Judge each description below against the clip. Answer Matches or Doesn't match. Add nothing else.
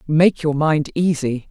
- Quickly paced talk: Doesn't match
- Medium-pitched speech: Matches